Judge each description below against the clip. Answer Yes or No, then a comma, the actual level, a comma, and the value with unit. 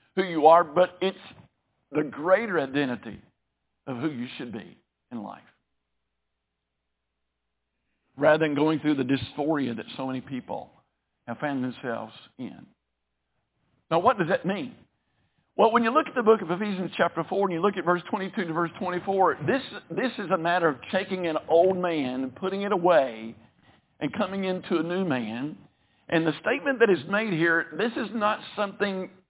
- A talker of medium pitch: Yes, medium, 170 Hz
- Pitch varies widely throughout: Yes, wide, 6.8 semitones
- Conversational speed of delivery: Yes, average, 180 wpm